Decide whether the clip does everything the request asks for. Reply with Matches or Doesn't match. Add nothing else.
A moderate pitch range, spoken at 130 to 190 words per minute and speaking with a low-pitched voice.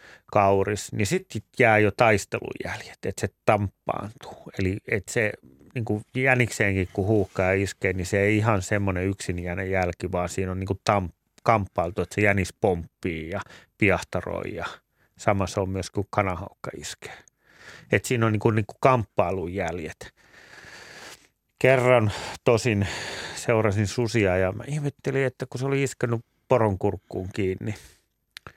Matches